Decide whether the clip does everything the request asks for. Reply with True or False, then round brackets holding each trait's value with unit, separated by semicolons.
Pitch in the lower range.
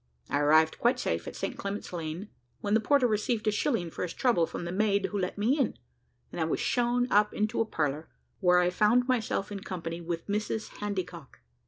False (205 Hz)